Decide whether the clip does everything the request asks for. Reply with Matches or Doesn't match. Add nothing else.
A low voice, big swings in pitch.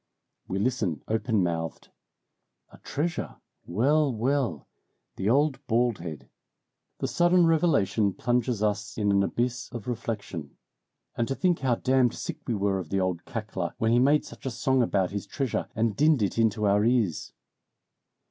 Doesn't match